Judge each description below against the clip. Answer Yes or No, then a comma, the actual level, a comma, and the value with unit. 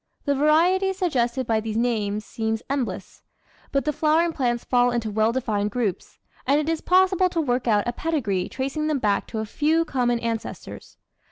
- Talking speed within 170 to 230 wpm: Yes, average, 185 wpm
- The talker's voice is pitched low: No, high, 245 Hz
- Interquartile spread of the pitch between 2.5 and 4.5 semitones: No, wide, 5.6 semitones